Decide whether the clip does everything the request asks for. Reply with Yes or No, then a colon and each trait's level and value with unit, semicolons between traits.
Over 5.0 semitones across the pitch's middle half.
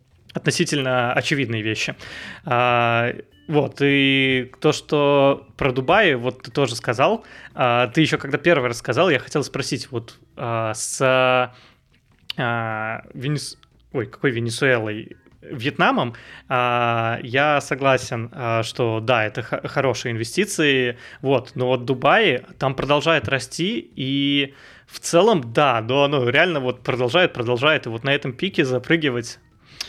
No: average, 3.0 semitones